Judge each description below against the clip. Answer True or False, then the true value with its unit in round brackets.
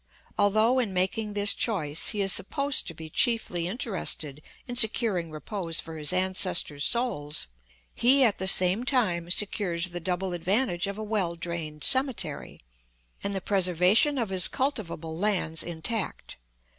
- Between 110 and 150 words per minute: True (145 wpm)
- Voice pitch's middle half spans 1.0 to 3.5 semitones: False (4.5 semitones)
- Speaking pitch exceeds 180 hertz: True (190 Hz)